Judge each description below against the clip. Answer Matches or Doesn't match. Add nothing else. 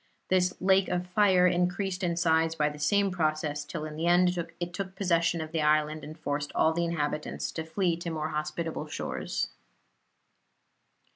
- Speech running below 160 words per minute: Doesn't match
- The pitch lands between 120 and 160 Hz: Doesn't match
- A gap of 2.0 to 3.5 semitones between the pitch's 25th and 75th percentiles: Matches